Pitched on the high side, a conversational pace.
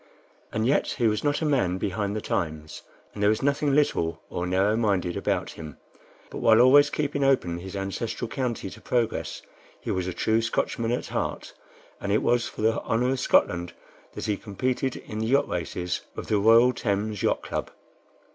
No: low, 110 Hz; average, 190 wpm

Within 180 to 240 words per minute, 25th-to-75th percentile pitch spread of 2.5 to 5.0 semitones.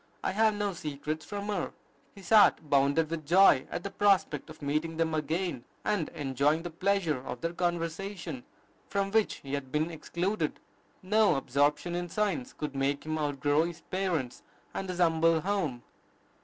No: average, 165 wpm; average, 4.7 semitones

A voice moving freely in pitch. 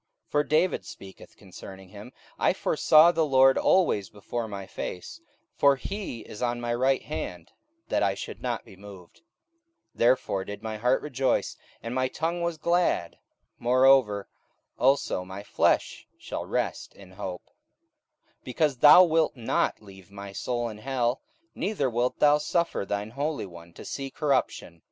Yes: wide, 6.0 semitones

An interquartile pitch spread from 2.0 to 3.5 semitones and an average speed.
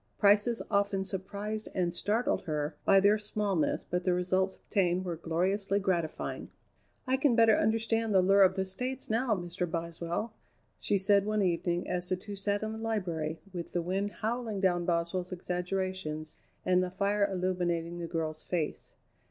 Yes: average, 2.9 semitones; average, 165 wpm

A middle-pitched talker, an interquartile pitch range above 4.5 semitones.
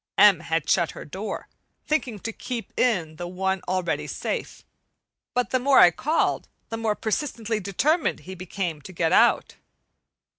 No: high, 200 Hz; average, 5.1 semitones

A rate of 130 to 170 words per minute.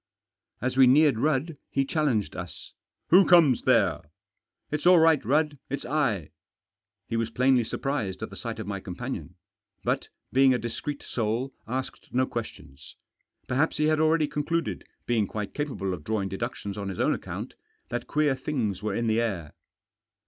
No: average, 180 wpm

